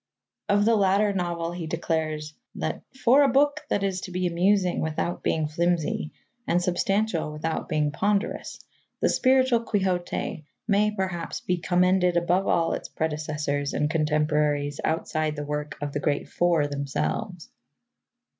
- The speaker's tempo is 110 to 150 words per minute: Yes, average, 145 wpm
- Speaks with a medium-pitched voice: Yes, medium, 170 Hz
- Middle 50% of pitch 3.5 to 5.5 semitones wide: Yes, average, 4.2 semitones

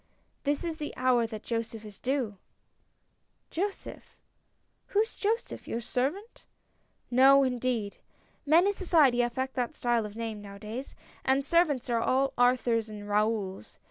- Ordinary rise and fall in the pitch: Yes, average, 4.0 semitones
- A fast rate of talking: No, average, 170 wpm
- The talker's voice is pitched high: Yes, very high, 250 Hz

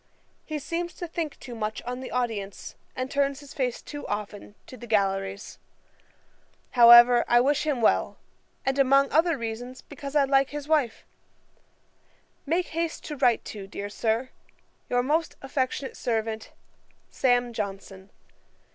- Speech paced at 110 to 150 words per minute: Yes, average, 145 wpm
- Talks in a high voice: Yes, very high, 250 Hz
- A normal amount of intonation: Yes, average, 4.2 semitones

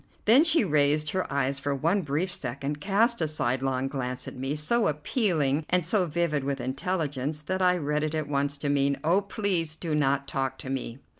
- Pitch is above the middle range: No, medium, 150 Hz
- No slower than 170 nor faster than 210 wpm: Yes, average, 200 wpm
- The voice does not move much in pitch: No, average, 4.4 semitones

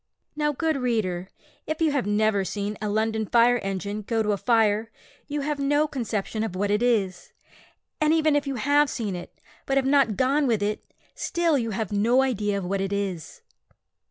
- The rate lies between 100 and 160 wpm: No, average, 195 wpm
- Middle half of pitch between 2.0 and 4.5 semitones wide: No, average, 5.2 semitones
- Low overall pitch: No, high, 225 Hz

